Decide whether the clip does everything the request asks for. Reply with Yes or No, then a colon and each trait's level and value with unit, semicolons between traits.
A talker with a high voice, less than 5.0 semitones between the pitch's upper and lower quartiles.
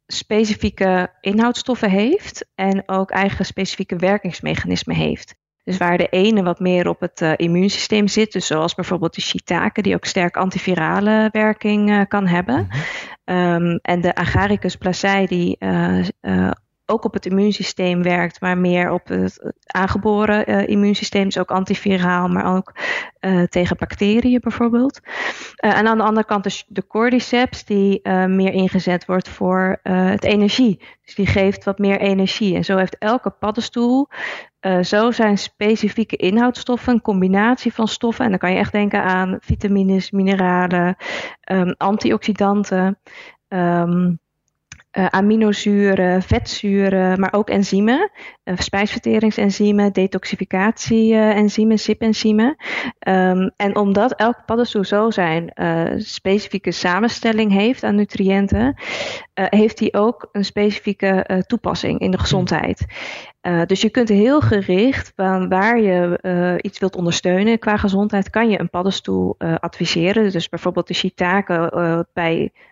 Yes: high, 195 Hz; average, 2.9 semitones